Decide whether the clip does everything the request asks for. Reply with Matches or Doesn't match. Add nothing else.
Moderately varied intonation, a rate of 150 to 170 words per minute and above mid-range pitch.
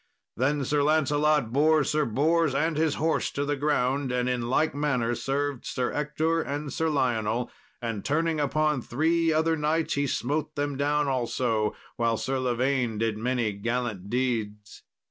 Doesn't match